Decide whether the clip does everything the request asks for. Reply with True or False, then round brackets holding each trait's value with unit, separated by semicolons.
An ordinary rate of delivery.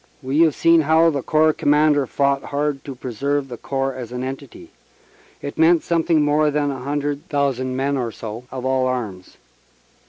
True (180 wpm)